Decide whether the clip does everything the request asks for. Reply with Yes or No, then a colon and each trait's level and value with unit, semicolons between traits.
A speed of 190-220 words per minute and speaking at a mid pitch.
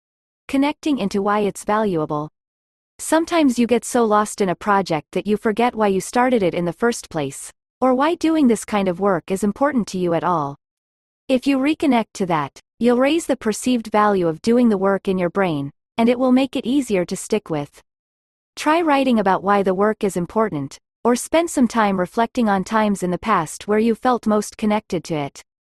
No: fast, 205 wpm; high, 210 Hz